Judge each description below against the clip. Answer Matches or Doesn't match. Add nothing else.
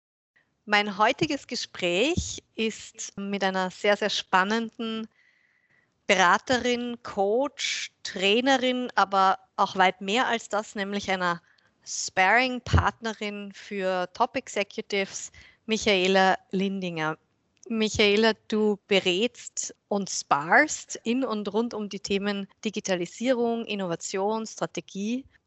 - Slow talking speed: Matches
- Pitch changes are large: Doesn't match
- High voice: Matches